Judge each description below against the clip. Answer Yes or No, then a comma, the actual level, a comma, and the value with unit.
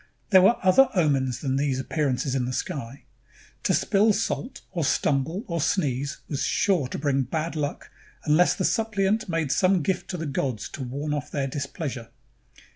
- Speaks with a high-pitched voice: No, medium, 150 Hz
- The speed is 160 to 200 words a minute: Yes, average, 180 wpm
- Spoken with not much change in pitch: No, average, 5.3 semitones